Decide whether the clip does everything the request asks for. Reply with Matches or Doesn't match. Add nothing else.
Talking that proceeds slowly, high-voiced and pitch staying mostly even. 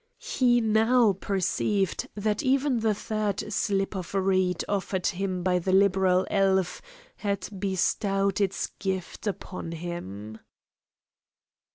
Matches